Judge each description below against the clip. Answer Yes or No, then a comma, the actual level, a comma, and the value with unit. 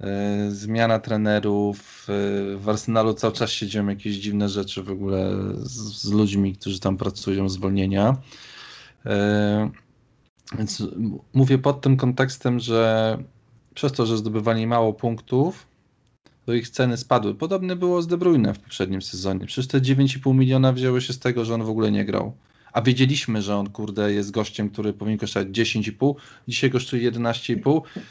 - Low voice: Yes, low, 110 Hz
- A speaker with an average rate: Yes, average, 150 wpm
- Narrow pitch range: No, average, 3.8 semitones